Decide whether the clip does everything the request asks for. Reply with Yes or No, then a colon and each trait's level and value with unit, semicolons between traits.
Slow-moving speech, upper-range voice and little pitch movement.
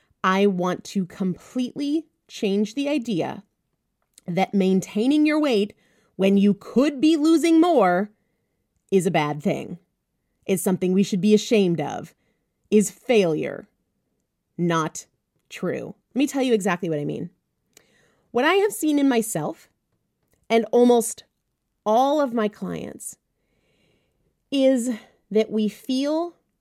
No: slow, 125 wpm; high, 215 Hz; wide, 5.6 semitones